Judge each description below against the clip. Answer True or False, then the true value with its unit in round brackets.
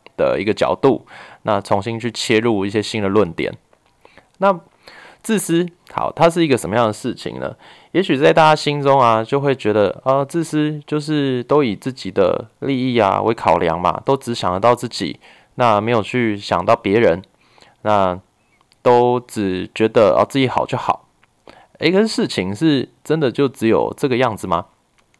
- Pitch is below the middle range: True (120 Hz)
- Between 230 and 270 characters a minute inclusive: True (250 characters per minute)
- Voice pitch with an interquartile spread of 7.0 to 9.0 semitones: False (5.3 semitones)